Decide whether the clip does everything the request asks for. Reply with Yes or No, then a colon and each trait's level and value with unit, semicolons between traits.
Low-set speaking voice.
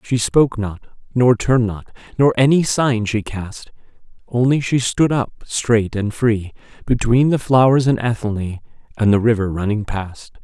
Yes: low, 115 Hz